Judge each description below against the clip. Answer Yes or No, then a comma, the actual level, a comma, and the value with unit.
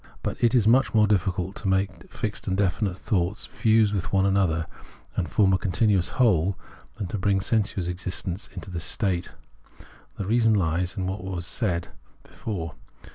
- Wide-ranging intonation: No, average, 2.8 semitones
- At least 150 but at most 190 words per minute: Yes, average, 170 wpm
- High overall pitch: No, very low, 95 Hz